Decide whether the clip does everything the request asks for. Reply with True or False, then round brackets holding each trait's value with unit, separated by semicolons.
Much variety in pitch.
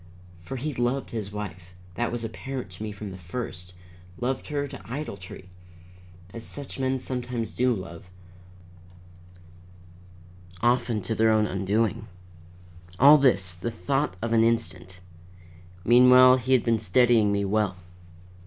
False (4.4 semitones)